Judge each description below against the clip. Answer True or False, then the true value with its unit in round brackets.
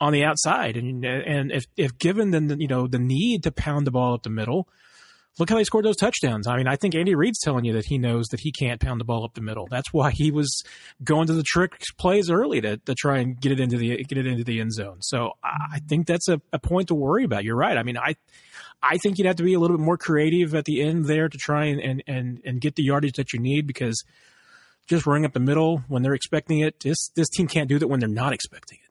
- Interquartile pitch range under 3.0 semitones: False (4.4 semitones)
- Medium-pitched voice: True (145 Hz)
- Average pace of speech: False (280 wpm)